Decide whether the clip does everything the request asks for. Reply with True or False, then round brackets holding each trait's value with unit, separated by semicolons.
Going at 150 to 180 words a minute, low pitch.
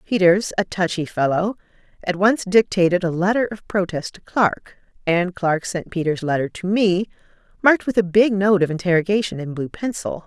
False (175 wpm; 185 Hz)